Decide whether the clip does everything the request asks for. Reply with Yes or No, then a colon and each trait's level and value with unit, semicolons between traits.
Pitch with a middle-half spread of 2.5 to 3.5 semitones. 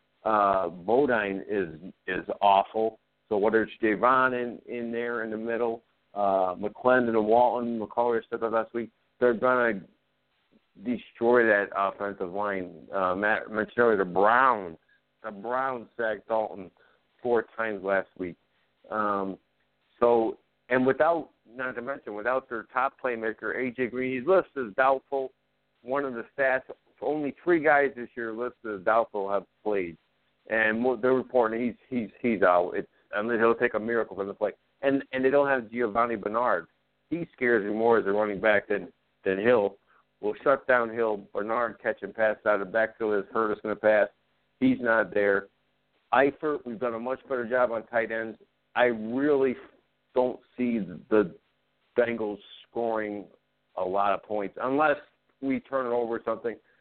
Yes: average, 3.1 semitones